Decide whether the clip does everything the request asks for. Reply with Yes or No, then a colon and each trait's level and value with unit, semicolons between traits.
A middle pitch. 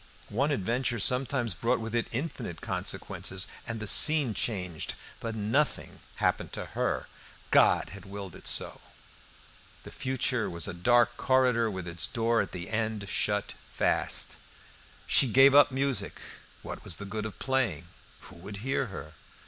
No: low, 115 Hz